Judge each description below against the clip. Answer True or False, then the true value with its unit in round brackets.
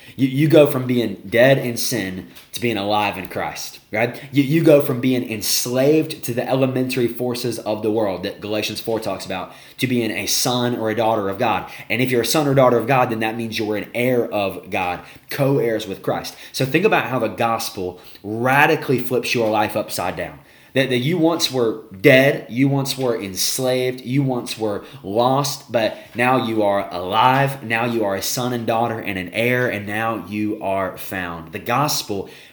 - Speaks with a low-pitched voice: True (120 Hz)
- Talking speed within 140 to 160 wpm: False (200 wpm)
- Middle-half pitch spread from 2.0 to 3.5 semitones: True (3.2 semitones)